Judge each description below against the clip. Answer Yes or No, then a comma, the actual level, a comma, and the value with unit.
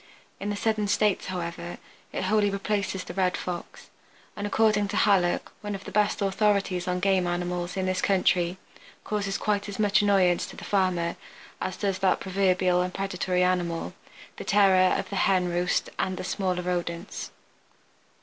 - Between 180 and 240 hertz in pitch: Yes, high, 190 Hz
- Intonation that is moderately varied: No, narrow, 2.0 semitones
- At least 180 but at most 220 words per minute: No, average, 170 wpm